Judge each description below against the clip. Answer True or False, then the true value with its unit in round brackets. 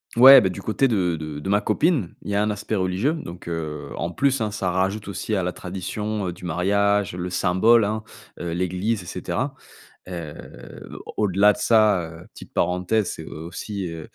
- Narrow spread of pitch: False (3.3 semitones)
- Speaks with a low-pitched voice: True (95 Hz)